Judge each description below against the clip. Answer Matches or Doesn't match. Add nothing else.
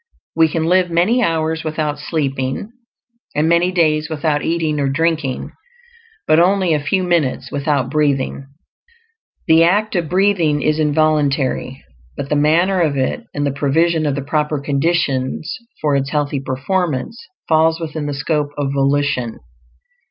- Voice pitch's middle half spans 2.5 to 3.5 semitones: Matches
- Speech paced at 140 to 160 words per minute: Matches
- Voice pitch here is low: Doesn't match